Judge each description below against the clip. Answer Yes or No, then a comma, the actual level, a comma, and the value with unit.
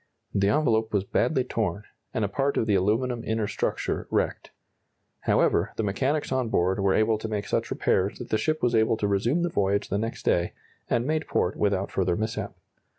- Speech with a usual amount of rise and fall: Yes, average, 3.6 semitones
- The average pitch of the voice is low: Yes, low, 110 Hz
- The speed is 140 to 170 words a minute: No, average, 200 wpm